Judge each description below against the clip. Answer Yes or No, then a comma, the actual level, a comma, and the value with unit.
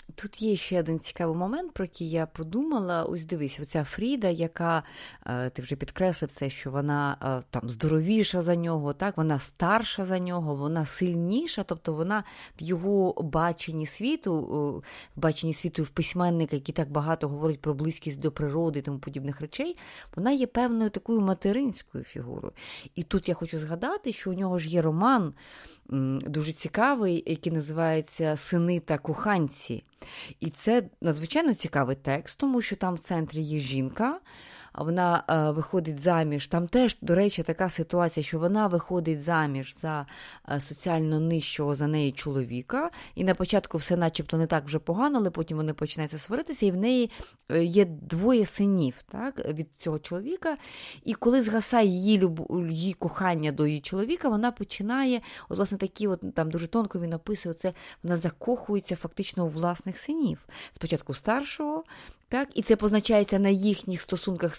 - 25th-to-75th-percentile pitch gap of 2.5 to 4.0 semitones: No, average, 4.5 semitones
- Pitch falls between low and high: Yes, medium, 170 Hz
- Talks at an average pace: No, fast, 160 wpm